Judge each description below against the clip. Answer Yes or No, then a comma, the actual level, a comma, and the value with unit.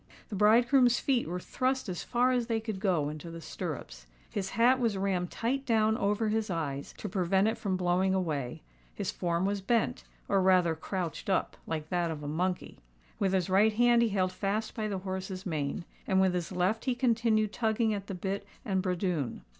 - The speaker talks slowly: No, average, 190 wpm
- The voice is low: No, high, 190 Hz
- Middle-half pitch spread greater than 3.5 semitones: Yes, average, 3.9 semitones